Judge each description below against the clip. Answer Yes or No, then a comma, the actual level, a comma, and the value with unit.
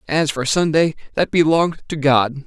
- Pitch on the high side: No, medium, 150 Hz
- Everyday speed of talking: Yes, average, 170 wpm